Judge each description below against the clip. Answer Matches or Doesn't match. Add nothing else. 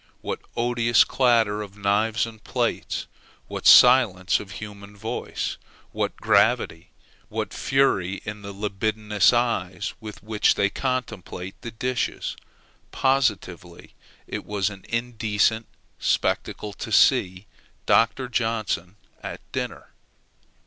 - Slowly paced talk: Matches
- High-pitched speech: Doesn't match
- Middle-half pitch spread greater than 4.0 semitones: Doesn't match